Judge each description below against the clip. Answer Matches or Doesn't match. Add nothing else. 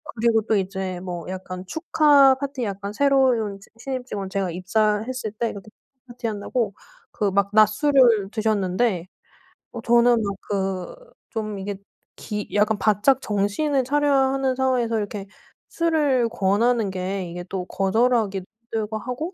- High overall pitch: Matches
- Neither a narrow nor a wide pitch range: Matches